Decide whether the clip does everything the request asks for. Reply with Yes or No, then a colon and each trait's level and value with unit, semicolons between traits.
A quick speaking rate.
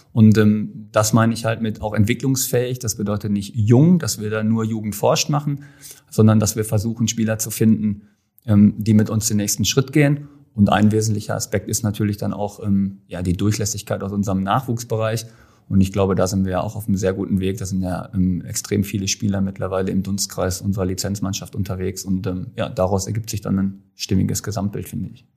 Yes: fast, 210 wpm